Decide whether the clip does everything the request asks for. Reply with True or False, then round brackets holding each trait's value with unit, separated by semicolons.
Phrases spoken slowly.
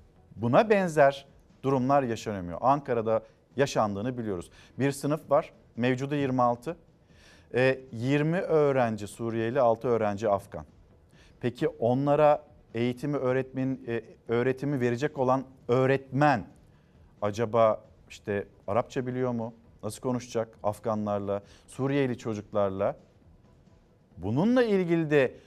True (90 wpm)